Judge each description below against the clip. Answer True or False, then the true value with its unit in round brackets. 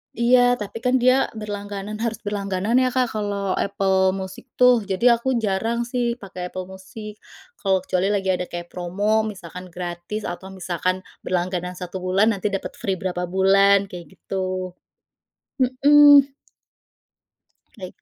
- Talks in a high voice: True (195 Hz)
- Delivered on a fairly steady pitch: False (3.5 semitones)